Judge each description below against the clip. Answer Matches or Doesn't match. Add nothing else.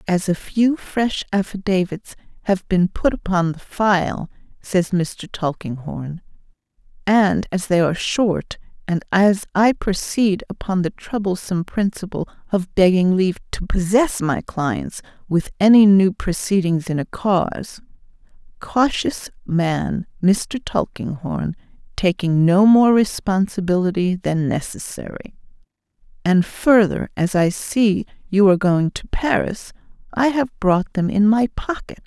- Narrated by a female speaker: Matches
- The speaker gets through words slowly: Matches